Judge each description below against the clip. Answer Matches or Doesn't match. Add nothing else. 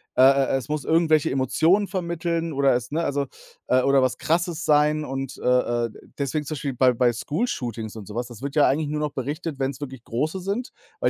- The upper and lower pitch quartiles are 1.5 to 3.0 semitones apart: Doesn't match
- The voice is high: Doesn't match